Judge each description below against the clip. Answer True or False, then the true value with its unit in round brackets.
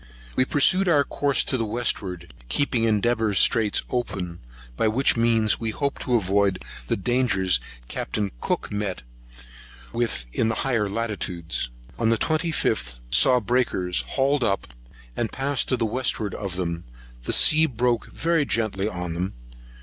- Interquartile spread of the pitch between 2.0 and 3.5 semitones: False (4.7 semitones)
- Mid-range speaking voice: False (115 Hz)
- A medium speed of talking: True (145 wpm)